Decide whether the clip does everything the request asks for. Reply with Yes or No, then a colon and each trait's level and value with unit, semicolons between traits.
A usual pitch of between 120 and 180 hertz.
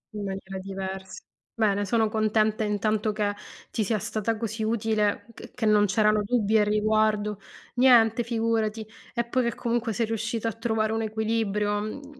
No: high, 215 Hz